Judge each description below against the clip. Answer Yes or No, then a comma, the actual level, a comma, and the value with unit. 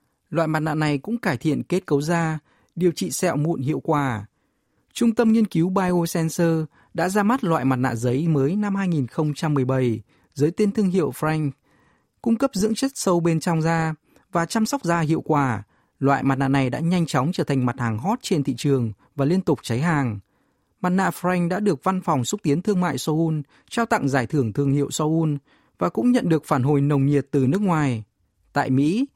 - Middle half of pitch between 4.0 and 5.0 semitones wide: Yes, average, 4.6 semitones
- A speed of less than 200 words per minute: No, average, 210 wpm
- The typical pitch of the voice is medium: Yes, medium, 155 Hz